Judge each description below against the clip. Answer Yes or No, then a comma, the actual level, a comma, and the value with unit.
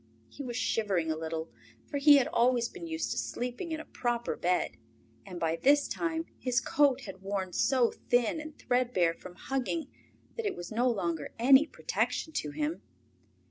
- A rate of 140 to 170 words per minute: No, average, 180 wpm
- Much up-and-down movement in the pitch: Yes, wide, 7.4 semitones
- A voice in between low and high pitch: No, high, 245 Hz